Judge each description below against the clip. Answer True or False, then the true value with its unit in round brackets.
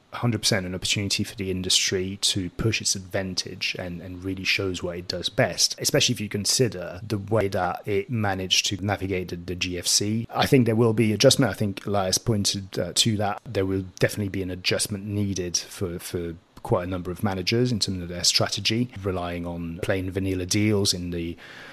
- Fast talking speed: False (195 wpm)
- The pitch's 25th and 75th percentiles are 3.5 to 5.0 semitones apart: False (3.0 semitones)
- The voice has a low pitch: True (100 Hz)